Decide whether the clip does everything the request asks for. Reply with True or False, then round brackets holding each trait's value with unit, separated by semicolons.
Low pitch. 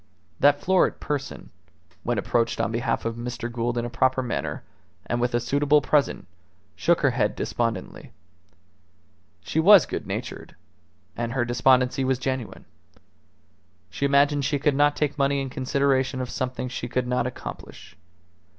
True (130 Hz)